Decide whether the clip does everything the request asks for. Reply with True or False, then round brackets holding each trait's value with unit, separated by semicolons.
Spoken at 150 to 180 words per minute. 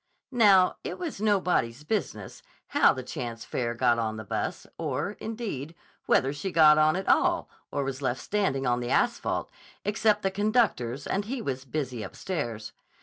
True (165 wpm)